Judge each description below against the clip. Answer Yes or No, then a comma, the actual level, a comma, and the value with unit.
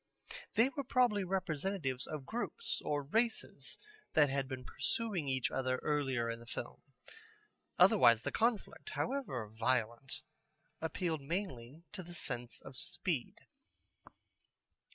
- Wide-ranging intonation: Yes, wide, 7.4 semitones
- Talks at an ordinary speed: No, slow, 120 wpm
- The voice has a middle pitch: Yes, medium, 150 Hz